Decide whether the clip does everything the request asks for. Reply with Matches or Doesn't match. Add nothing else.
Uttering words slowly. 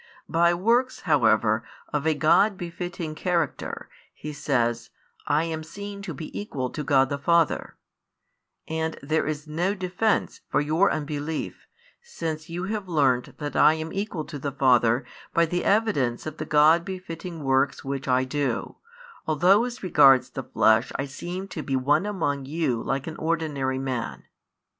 Doesn't match